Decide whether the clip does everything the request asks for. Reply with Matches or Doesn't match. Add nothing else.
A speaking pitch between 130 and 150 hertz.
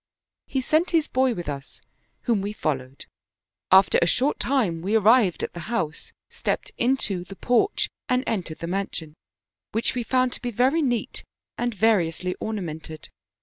Doesn't match